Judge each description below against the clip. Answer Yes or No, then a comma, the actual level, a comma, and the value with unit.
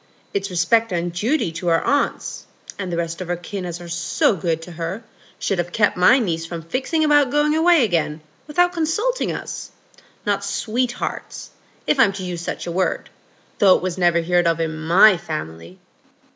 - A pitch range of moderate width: No, wide, 5.8 semitones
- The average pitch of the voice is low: No, medium, 180 Hz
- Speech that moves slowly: No, average, 185 wpm